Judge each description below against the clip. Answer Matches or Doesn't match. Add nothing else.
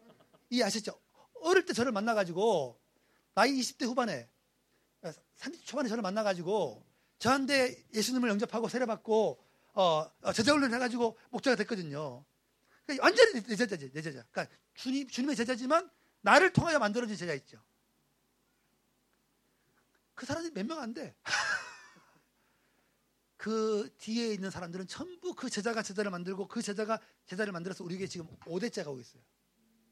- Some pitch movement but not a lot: Matches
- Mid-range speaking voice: Doesn't match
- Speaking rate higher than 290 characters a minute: Matches